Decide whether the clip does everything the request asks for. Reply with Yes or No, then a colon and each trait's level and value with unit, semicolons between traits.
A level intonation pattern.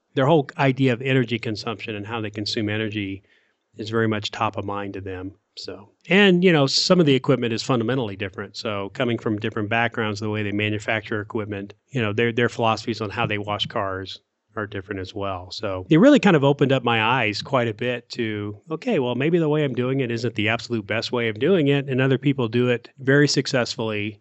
No: average, 3.9 semitones